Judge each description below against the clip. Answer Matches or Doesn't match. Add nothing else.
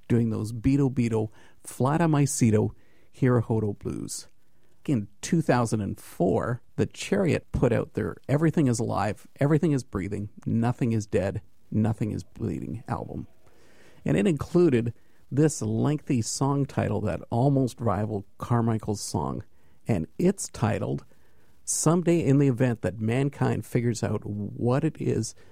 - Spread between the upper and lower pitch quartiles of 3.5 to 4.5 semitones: Matches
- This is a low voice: Matches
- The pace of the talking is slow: Matches